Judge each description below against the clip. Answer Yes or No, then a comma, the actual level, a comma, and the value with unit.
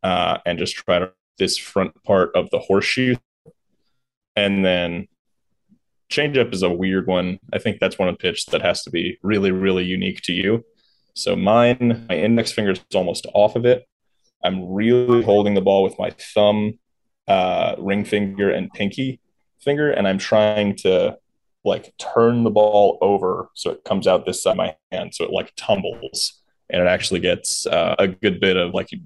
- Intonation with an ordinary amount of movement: Yes, average, 3.5 semitones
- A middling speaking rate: Yes, average, 190 wpm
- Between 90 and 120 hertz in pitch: Yes, low, 105 Hz